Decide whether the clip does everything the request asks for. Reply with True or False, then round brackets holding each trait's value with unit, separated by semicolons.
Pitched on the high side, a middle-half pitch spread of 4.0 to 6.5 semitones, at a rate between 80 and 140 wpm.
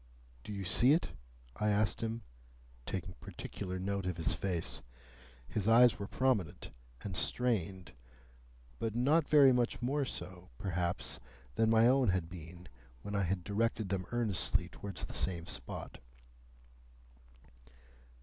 False (100 Hz; 4.3 semitones; 135 wpm)